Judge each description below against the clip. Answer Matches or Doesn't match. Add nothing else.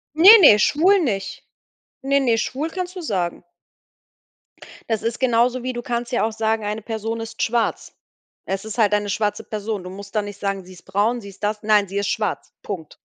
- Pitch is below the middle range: Doesn't match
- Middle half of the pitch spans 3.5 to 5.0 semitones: Doesn't match